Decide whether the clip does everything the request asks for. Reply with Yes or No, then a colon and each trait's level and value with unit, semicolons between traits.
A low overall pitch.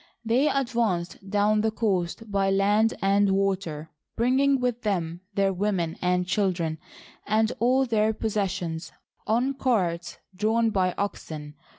No: high, 200 Hz